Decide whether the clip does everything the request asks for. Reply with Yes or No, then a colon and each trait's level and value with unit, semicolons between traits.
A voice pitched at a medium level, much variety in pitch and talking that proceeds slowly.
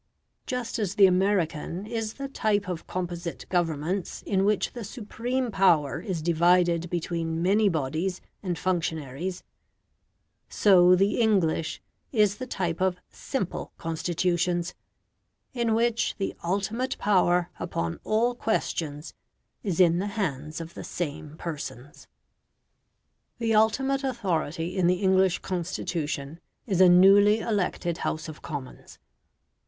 No: medium, 180 Hz; average, 3.9 semitones; slow, 125 wpm